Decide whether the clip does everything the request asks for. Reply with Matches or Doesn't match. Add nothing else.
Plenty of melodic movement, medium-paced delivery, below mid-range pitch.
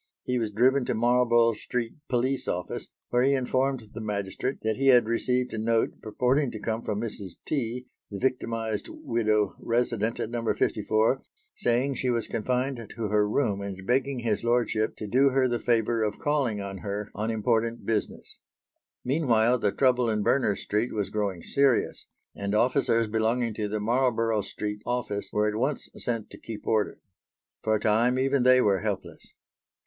Doesn't match